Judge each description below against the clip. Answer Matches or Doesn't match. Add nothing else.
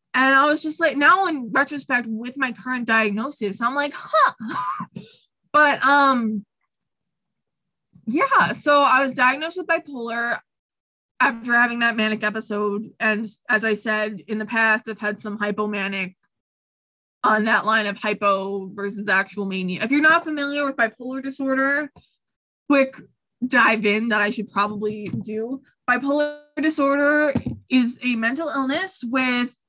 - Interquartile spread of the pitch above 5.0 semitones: Doesn't match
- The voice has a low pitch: Doesn't match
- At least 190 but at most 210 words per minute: Doesn't match